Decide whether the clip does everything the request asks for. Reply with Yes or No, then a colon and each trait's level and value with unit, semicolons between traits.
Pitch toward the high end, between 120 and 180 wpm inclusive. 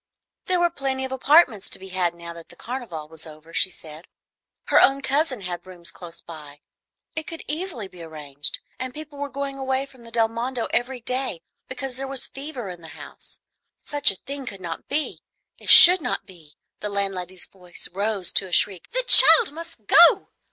No: high, 230 Hz; average, 195 wpm